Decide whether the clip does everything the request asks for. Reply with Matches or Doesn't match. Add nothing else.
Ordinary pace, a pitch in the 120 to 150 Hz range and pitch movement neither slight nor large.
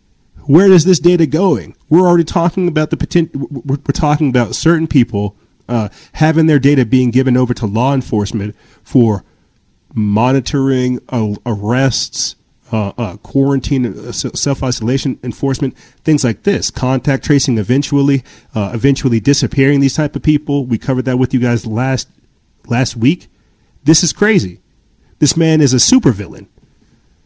Matches